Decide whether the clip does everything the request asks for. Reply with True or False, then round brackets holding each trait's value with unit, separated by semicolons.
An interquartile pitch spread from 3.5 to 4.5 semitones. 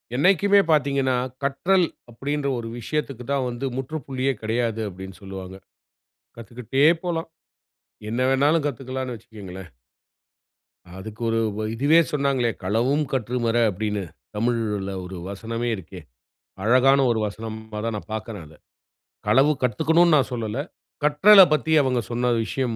True (4.2 semitones)